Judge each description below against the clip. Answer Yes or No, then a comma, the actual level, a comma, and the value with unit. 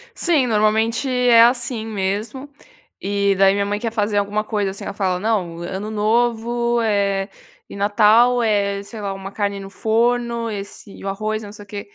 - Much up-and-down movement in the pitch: No, narrow, 2.6 semitones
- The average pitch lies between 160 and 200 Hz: No, high, 210 Hz